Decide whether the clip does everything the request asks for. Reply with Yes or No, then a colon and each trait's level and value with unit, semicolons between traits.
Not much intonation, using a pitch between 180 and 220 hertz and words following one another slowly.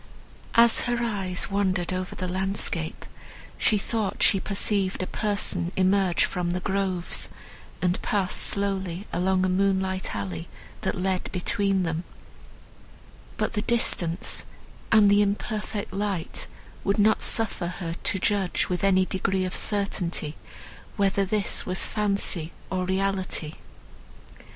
Yes: narrow, 1.8 semitones; high, 190 Hz; slow, 125 wpm